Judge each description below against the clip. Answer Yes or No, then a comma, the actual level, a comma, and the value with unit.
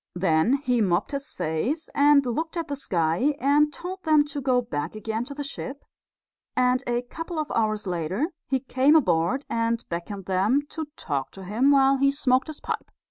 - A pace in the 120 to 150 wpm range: No, average, 190 wpm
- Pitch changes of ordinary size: No, wide, 6.7 semitones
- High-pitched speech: Yes, very high, 255 Hz